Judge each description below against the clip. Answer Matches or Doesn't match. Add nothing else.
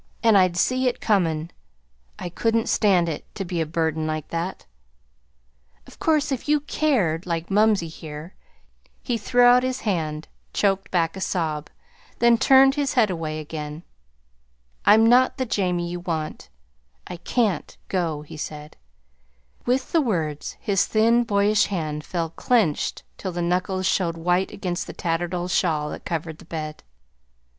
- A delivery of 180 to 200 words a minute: Doesn't match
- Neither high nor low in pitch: Matches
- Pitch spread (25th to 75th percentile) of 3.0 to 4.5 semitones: Doesn't match